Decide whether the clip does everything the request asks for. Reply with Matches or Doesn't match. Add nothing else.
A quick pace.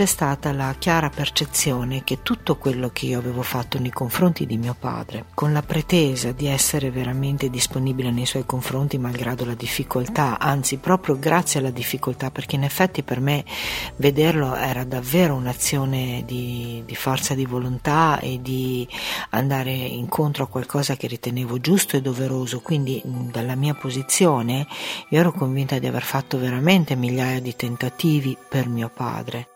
Doesn't match